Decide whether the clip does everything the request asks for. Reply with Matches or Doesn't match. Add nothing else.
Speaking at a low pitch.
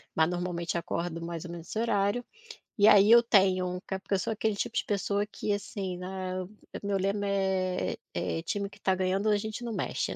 Doesn't match